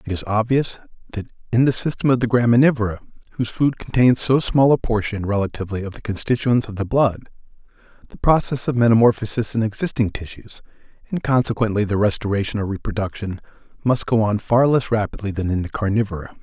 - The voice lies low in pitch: Yes, low, 110 Hz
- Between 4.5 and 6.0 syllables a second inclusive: No, 6.2 syllables/s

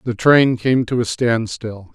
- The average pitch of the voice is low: Yes, low, 115 Hz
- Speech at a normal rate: Yes, average, 185 wpm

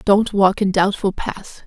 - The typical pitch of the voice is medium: No, high, 195 Hz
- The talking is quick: No, average, 180 wpm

